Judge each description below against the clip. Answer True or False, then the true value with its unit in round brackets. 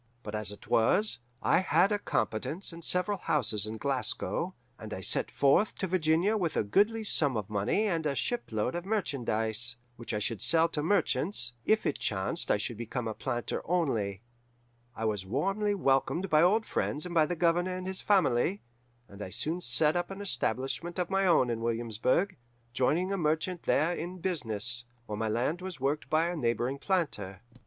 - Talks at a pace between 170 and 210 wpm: True (190 wpm)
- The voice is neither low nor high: True (150 Hz)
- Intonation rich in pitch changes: True (7.8 semitones)